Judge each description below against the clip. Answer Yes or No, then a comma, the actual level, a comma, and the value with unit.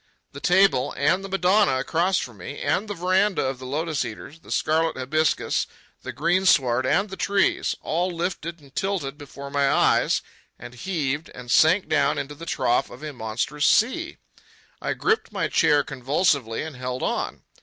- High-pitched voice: No, medium, 150 Hz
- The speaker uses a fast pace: No, average, 165 wpm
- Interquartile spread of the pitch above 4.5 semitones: Yes, average, 5.3 semitones